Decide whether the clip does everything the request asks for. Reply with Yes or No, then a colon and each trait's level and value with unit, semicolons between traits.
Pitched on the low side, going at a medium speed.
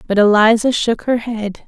No: high, 220 Hz; average, 180 wpm